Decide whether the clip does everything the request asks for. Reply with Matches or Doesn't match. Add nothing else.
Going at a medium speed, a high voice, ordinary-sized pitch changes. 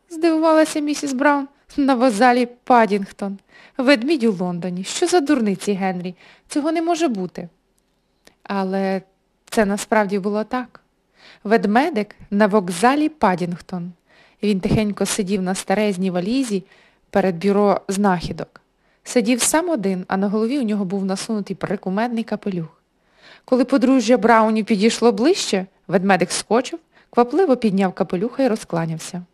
Matches